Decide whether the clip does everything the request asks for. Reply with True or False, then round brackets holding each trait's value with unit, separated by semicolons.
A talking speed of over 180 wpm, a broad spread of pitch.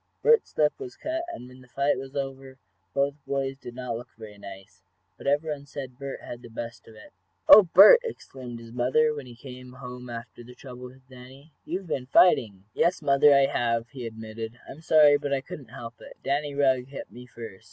False (205 wpm; 2.9 semitones)